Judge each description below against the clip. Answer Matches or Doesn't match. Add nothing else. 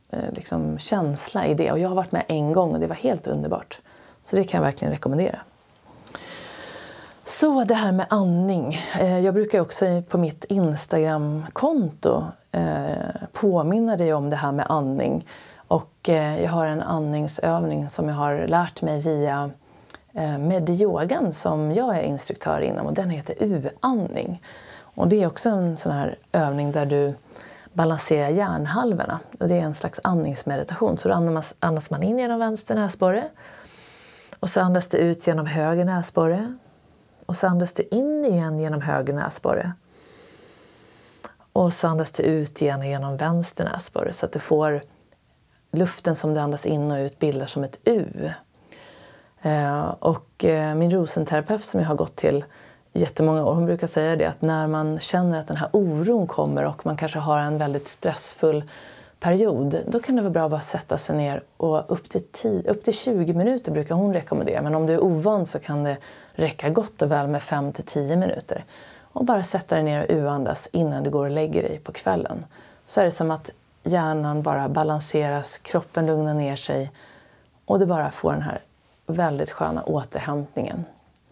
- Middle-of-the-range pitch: Matches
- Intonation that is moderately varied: Matches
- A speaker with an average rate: Matches